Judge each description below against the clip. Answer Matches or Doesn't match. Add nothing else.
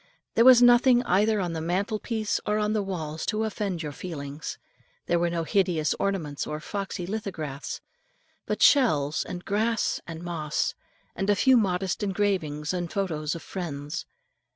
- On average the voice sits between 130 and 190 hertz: Matches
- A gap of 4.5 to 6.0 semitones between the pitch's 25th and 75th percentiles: Matches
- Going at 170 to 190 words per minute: Doesn't match